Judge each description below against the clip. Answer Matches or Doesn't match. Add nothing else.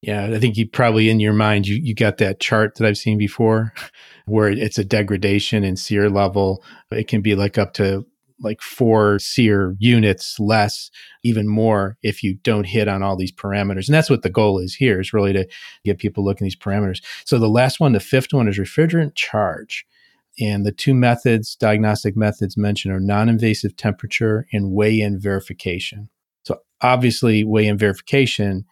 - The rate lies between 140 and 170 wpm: Doesn't match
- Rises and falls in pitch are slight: Matches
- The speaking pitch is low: Matches